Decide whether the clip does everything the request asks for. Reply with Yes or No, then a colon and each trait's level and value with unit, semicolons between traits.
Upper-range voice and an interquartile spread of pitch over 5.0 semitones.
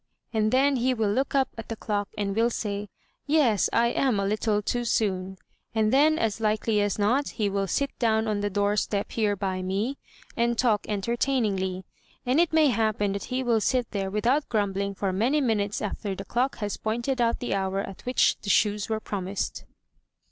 No: high, 215 Hz; average, 3.1 semitones